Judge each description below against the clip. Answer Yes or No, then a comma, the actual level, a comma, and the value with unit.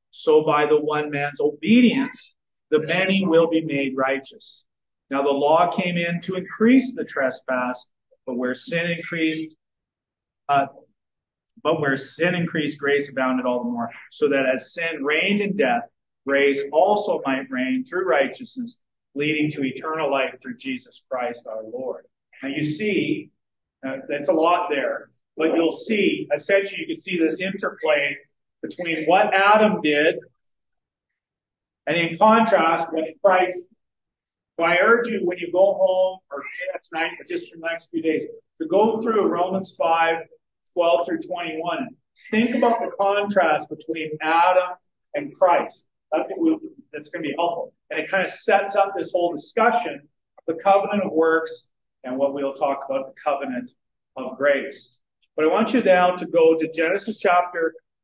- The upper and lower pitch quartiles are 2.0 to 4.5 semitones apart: No, wide, 5.6 semitones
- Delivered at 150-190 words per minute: Yes, average, 160 wpm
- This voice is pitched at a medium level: Yes, medium, 165 Hz